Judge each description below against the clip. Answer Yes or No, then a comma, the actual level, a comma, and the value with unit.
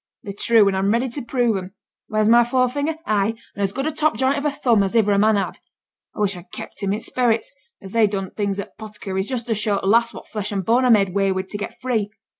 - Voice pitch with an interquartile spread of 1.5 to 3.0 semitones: No, average, 3.4 semitones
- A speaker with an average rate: No, fast, 270 wpm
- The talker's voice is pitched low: No, high, 215 Hz